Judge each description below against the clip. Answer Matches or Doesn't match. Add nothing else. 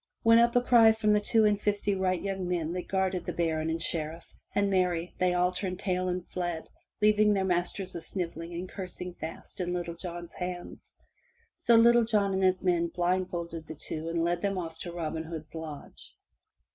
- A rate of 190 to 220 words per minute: Matches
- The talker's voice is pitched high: Doesn't match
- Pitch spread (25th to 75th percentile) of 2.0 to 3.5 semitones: Matches